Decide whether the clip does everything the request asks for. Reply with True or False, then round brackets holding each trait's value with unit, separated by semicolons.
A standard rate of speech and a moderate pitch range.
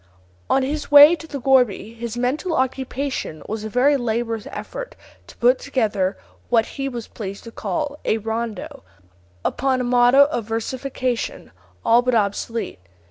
True (150 wpm; 3.3 semitones)